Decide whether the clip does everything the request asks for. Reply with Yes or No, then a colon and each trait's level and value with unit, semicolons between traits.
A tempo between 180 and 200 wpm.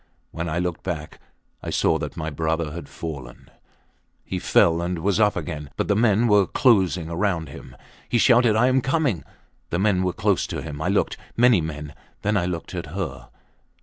Yes: average, 190 wpm